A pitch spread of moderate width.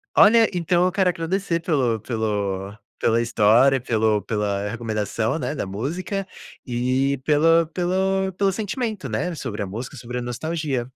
No: wide, 8.1 semitones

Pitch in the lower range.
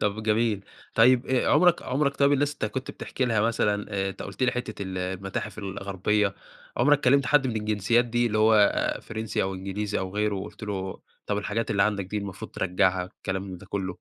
Yes: low, 105 Hz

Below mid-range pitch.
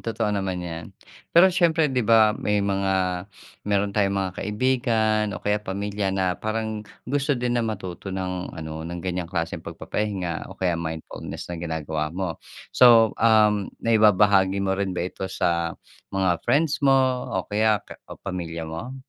Yes: low, 100 Hz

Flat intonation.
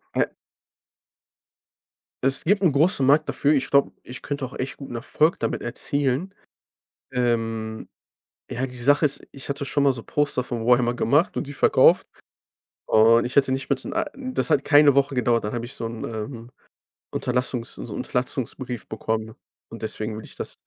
No: average, 3.4 semitones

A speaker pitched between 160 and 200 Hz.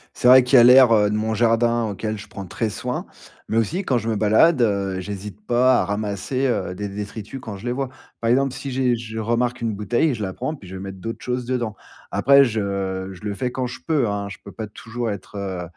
No: low, 110 Hz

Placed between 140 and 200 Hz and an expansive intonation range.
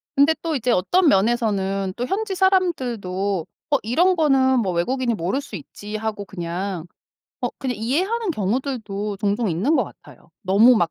No: high, 225 Hz; wide, 6.1 semitones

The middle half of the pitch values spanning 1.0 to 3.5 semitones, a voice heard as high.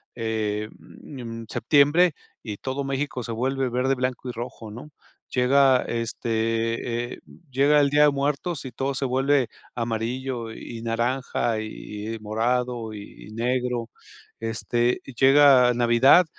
No: average, 2.8 semitones; low, 125 Hz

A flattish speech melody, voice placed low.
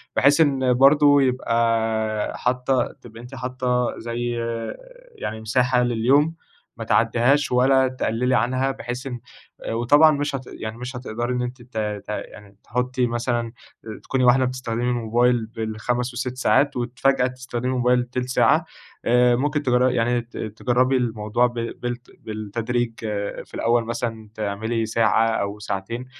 Yes: narrow, 1.9 semitones; low, 120 Hz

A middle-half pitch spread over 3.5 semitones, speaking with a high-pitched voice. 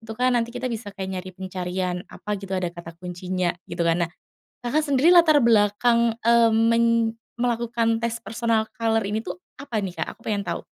Yes: average, 3.9 semitones; high, 220 Hz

